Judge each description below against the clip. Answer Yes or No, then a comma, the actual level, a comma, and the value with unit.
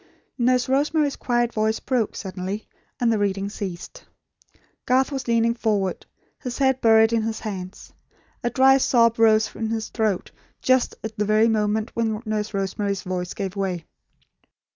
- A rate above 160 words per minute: No, average, 155 wpm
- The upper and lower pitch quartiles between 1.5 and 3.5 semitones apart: Yes, average, 2.9 semitones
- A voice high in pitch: Yes, high, 220 Hz